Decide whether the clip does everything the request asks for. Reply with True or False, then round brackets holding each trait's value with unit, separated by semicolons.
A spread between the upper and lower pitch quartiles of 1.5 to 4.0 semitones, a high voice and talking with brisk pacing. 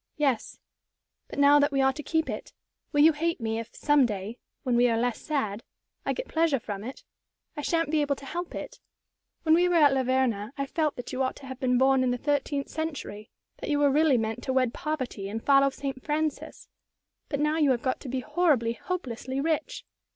True (3.5 semitones; 275 Hz; 220 wpm)